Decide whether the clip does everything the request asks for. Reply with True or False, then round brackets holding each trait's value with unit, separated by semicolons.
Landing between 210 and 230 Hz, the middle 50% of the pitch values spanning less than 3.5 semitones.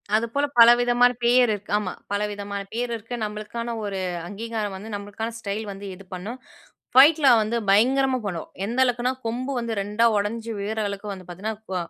True (220 Hz; 3.0 semitones)